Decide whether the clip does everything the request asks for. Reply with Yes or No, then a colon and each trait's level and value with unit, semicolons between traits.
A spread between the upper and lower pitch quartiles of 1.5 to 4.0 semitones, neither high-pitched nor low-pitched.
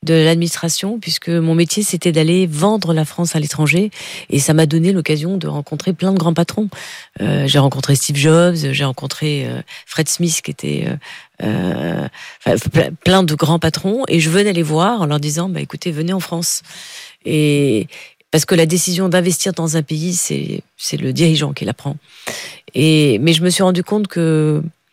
Yes: average, 2.8 semitones; medium, 165 Hz